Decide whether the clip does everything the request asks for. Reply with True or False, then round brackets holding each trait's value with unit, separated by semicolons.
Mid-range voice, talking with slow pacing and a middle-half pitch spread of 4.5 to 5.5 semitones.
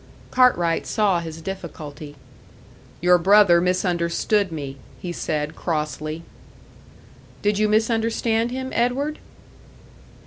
True (180 Hz; 95 wpm; 5.2 semitones)